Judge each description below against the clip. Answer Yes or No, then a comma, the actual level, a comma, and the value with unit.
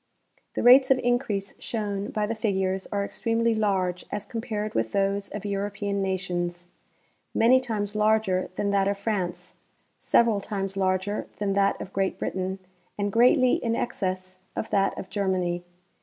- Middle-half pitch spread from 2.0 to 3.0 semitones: Yes, narrow, 2.4 semitones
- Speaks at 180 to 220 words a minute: No, average, 155 wpm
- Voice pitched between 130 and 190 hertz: No, high, 200 Hz